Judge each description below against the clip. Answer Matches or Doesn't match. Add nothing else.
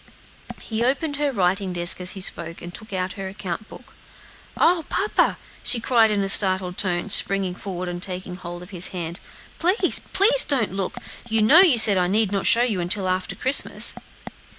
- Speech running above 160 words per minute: Matches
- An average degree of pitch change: Matches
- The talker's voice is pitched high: Matches